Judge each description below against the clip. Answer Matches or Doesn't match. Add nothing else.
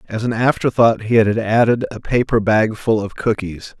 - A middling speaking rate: Matches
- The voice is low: Matches